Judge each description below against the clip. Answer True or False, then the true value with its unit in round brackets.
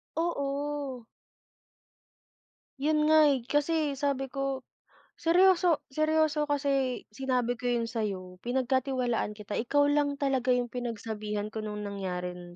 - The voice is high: True (265 Hz)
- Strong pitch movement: False (4.5 semitones)